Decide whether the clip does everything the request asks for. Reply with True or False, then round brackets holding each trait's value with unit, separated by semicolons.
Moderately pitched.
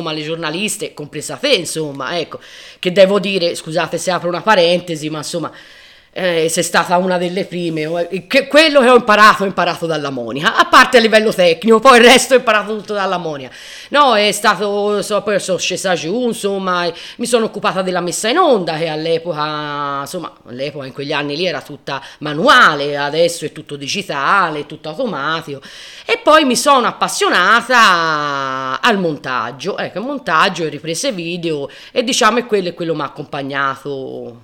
True (175 Hz)